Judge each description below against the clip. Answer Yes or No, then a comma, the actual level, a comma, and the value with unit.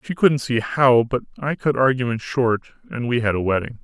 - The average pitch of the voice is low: Yes, low, 125 Hz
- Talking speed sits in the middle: No, fast, 220 wpm